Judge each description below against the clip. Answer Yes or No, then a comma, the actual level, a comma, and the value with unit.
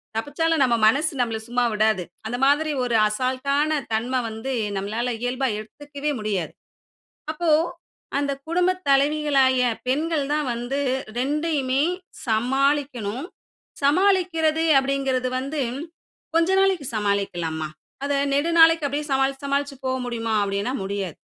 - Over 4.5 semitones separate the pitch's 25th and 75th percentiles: No, average, 4.1 semitones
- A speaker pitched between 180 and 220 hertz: No, very high, 270 Hz